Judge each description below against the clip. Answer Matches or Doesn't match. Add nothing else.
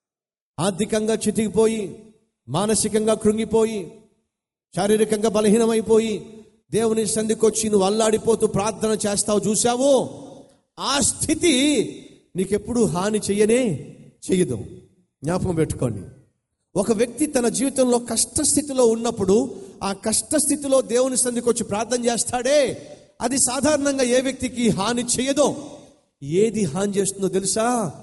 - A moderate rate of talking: Matches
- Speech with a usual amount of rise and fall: Matches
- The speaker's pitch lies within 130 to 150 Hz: Doesn't match